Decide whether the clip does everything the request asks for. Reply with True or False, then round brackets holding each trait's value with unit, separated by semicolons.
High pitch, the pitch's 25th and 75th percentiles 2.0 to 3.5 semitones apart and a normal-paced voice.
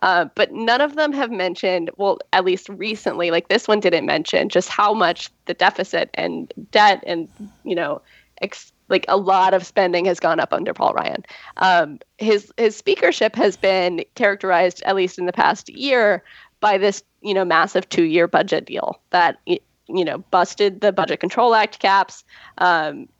True (195 Hz; 2.8 semitones; 180 wpm)